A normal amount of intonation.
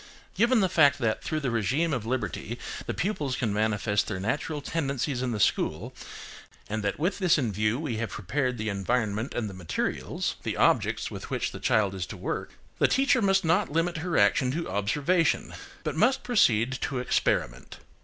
No: wide, 7.1 semitones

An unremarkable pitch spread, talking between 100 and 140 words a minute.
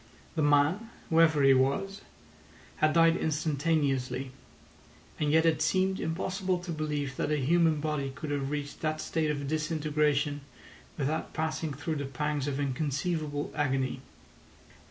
No: narrow, 2.2 semitones; slow, 135 wpm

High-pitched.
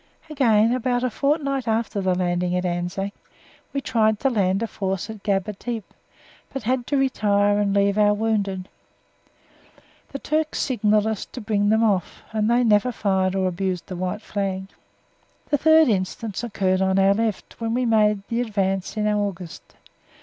Yes: high, 210 Hz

